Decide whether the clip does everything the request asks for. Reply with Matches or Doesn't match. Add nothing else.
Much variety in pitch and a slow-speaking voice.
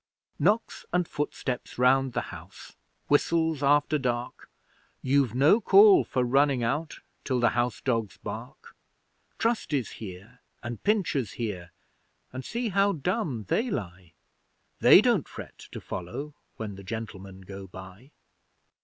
Matches